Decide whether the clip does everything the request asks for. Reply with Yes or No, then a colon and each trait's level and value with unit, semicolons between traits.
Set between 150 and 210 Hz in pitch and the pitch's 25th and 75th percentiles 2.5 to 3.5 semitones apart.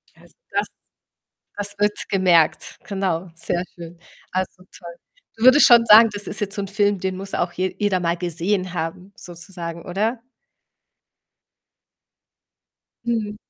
Yes: high, 190 Hz; average, 2.9 semitones